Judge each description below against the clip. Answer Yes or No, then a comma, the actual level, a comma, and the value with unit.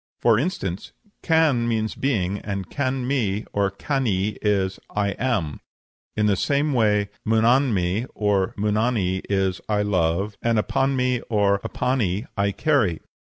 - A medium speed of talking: No, slow, 130 wpm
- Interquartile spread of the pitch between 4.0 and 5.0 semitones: Yes, average, 4.3 semitones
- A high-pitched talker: No, low, 105 Hz